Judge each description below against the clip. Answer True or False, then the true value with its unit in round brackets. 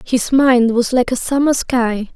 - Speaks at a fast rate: False (195 wpm)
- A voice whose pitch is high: True (245 Hz)